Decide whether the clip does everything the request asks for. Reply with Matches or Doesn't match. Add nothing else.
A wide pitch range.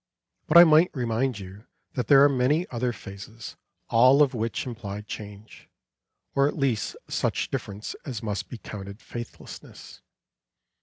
Doesn't match